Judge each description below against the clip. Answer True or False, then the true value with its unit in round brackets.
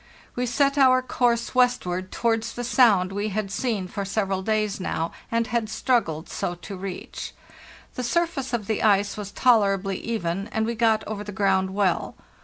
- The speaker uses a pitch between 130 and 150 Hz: False (215 Hz)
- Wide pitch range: False (3.4 semitones)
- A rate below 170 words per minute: False (175 wpm)